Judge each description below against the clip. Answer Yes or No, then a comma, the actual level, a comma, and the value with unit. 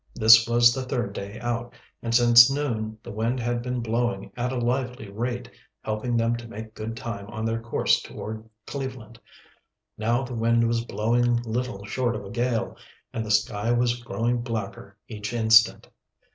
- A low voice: Yes, low, 115 Hz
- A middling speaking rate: Yes, average, 175 wpm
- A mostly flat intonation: Yes, narrow, 1.6 semitones